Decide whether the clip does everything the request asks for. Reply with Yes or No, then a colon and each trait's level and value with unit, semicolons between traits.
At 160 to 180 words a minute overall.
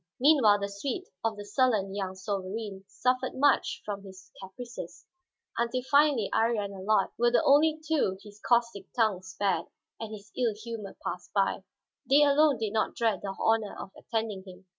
Yes: average, 170 wpm